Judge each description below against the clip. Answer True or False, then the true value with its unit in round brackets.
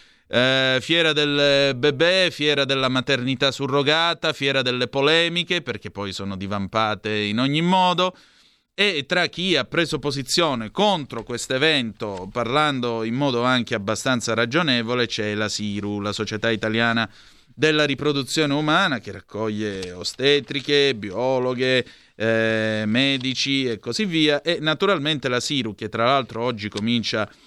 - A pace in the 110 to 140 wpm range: True (130 wpm)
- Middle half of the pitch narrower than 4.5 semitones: False (4.8 semitones)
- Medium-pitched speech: False (130 Hz)